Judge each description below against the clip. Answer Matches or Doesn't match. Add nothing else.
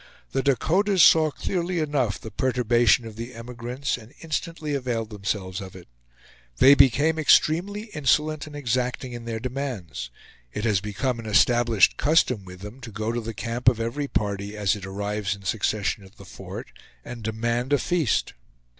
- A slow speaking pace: Doesn't match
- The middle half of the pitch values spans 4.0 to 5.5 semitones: Matches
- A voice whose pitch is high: Doesn't match